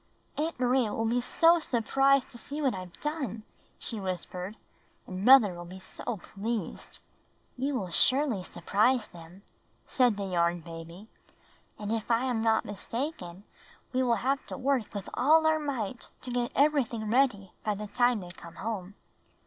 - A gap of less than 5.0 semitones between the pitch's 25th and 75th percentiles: No, average, 5.3 semitones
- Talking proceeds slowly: No, average, 165 wpm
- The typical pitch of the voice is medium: No, high, 225 Hz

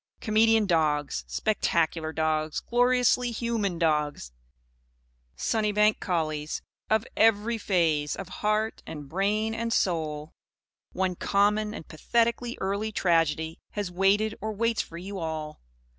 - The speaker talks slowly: Yes, slow, 115 wpm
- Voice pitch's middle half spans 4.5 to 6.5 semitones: Yes, average, 5.3 semitones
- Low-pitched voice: No, high, 195 Hz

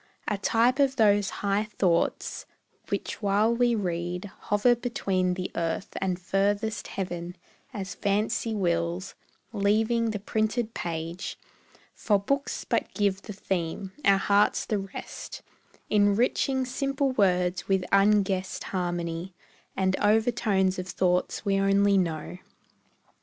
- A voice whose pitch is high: Yes, high, 200 Hz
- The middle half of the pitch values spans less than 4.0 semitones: Yes, average, 2.9 semitones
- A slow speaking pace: Yes, slow, 120 wpm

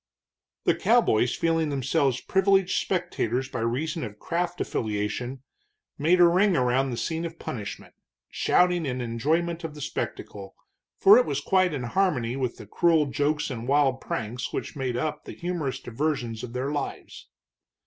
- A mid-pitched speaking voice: Yes, medium, 145 Hz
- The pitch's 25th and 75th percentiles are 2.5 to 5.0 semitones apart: No, wide, 5.5 semitones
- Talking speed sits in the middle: Yes, average, 160 wpm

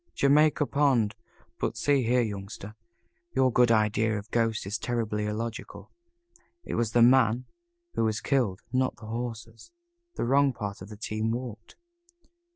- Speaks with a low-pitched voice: Yes, low, 115 Hz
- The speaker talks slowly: No, average, 145 wpm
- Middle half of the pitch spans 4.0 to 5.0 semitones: No, average, 2.9 semitones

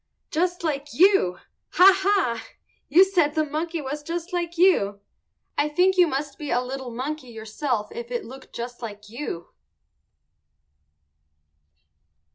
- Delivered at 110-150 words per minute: Yes, average, 140 wpm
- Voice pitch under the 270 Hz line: No, very high, 295 Hz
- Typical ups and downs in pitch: No, wide, 6.2 semitones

